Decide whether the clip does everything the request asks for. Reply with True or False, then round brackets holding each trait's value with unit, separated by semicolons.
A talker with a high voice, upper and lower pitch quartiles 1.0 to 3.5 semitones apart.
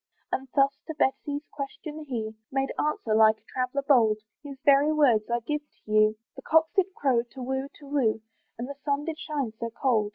False (270 Hz; 4.0 semitones)